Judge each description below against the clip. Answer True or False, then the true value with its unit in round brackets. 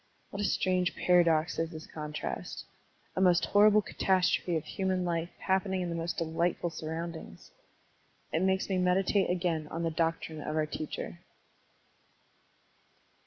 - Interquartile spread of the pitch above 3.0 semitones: False (2.5 semitones)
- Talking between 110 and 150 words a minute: True (145 wpm)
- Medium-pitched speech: True (170 Hz)